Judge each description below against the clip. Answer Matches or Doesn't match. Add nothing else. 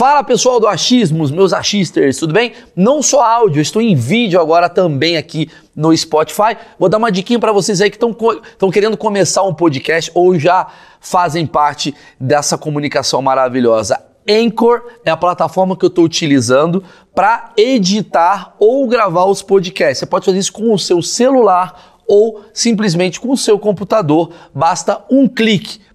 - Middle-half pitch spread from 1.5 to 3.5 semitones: Doesn't match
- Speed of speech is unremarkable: Matches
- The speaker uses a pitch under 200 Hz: Matches